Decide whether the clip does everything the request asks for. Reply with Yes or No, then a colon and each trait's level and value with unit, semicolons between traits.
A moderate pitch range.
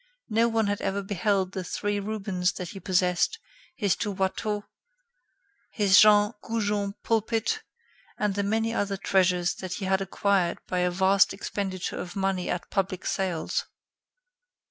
No: narrow, 1.9 semitones